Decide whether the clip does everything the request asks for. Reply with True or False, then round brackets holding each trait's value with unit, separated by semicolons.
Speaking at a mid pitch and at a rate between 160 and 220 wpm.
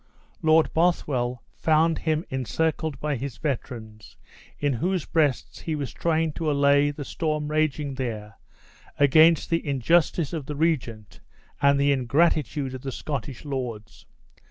False (145 Hz; 135 wpm)